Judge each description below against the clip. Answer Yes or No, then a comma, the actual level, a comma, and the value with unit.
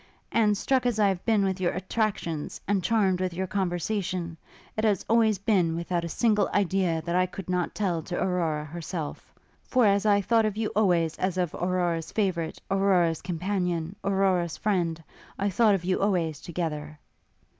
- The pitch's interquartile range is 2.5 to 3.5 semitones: Yes, average, 3.0 semitones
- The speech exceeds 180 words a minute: No, average, 175 wpm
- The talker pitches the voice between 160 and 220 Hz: Yes, medium, 185 Hz